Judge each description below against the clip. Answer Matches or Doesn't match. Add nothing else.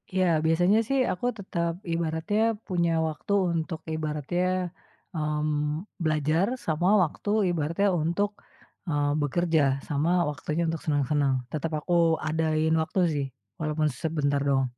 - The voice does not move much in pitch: Matches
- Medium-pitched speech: Matches